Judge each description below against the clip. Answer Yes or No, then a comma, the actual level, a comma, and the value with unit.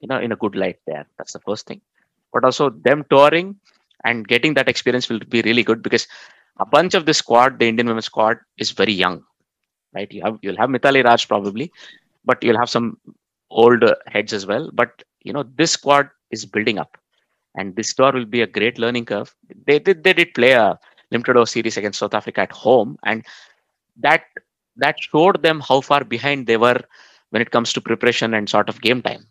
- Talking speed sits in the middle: No, fast, 215 wpm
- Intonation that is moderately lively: Yes, average, 3.7 semitones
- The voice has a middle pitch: No, low, 120 Hz